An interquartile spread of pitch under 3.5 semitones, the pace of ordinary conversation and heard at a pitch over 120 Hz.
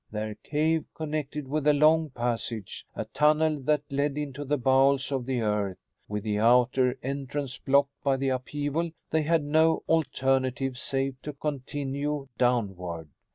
Yes: average, 2.9 semitones; average, 150 wpm; low, 135 Hz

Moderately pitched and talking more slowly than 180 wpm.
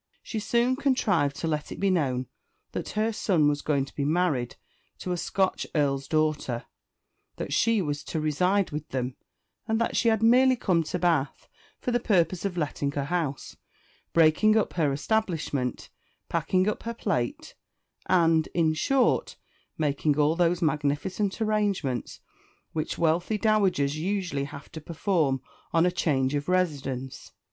Yes: medium, 165 Hz; average, 155 wpm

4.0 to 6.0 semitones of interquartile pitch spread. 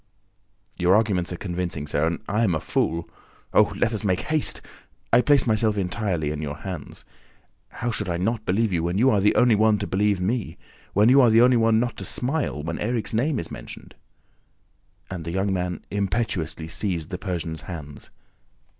Yes: average, 4.7 semitones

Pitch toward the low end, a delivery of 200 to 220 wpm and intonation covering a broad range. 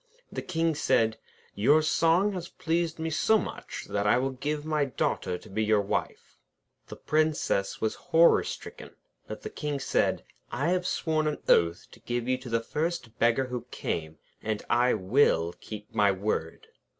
No: low, 130 Hz; average, 175 wpm; wide, 6.7 semitones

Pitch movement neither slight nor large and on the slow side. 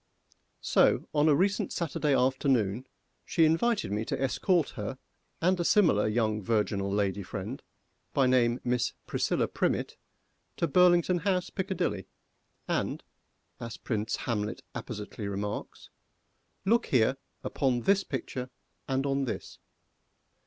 No: wide, 8.0 semitones; slow, 125 wpm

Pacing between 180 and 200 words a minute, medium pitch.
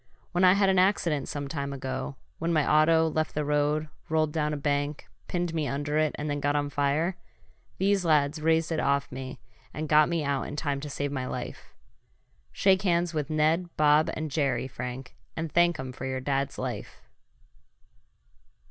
Yes: average, 185 wpm; medium, 150 Hz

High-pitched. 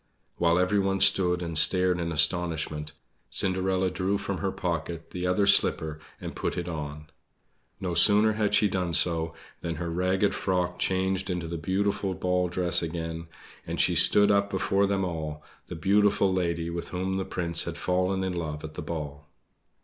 No: very low, 90 Hz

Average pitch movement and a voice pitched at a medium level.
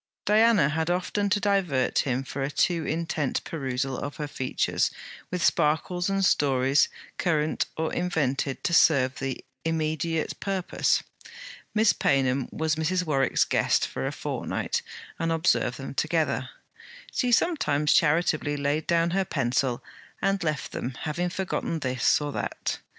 Yes: average, 4.2 semitones; medium, 155 Hz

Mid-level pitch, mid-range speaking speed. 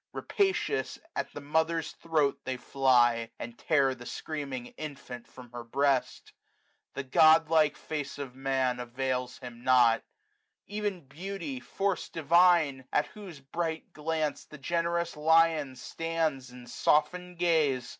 No: medium, 145 Hz; slow, 130 wpm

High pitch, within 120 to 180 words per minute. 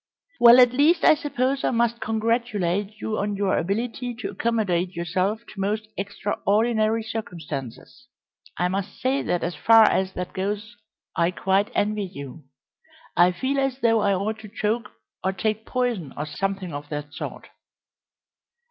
Yes: high, 210 Hz; average, 155 wpm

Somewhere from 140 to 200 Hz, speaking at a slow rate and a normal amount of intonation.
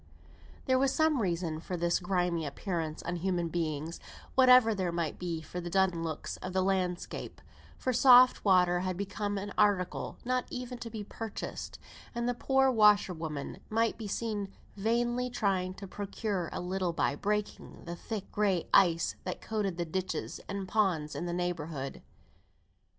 No: high, 190 Hz; average, 160 wpm; average, 4.1 semitones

